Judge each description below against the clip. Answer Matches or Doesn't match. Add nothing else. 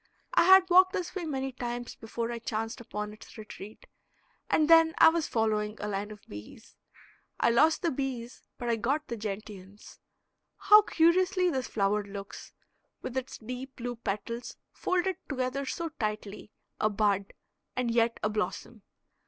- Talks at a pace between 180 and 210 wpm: Doesn't match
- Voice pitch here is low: Doesn't match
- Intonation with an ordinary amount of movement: Doesn't match